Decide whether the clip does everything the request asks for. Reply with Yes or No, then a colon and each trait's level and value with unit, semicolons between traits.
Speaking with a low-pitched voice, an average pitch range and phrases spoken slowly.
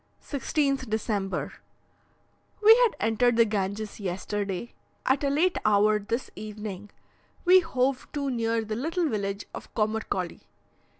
No: high, 225 Hz; average, 4.9 semitones; slow, 125 wpm